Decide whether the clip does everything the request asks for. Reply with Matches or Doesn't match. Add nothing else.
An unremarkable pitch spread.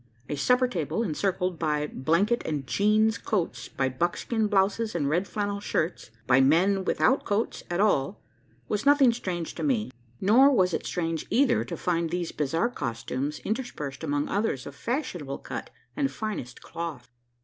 Doesn't match